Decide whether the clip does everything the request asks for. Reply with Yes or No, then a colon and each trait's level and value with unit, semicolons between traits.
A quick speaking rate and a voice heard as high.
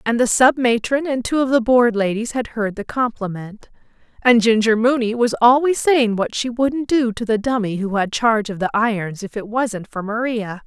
Yes: fast, 215 wpm; high, 230 Hz